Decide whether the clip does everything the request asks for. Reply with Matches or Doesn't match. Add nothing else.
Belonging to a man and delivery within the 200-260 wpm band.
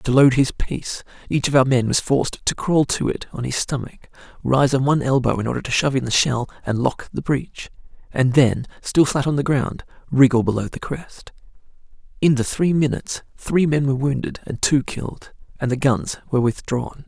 Matches